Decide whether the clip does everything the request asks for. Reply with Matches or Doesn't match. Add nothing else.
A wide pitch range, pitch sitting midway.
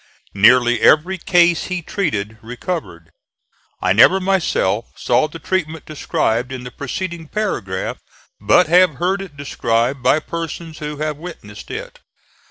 Matches